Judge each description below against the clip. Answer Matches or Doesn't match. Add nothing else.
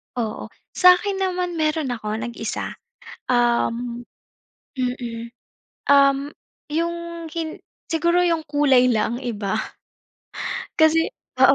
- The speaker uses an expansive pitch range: Matches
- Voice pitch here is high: Matches